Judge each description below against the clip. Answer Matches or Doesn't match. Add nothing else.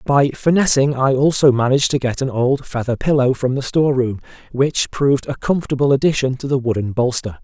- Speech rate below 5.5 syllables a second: Doesn't match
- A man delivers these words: Matches